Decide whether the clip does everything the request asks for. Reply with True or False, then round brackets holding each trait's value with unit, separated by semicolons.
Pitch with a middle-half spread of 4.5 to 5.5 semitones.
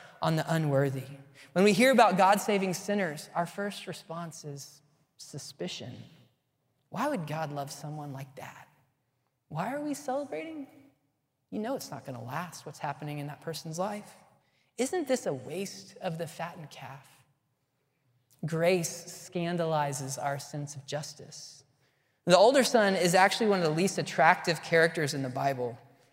True (5.1 semitones)